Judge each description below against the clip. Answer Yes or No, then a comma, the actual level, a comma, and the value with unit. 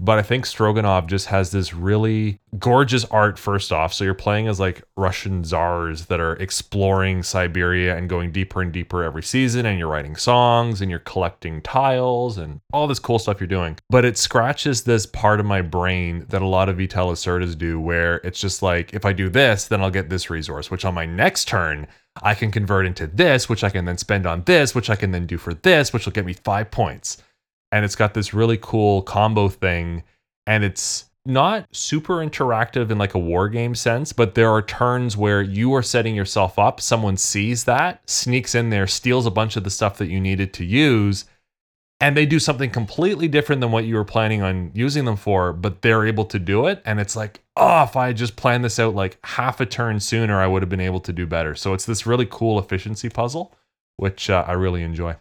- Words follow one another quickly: Yes, fast, 225 wpm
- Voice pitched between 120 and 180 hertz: No, low, 100 Hz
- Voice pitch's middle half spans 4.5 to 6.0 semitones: No, average, 4.0 semitones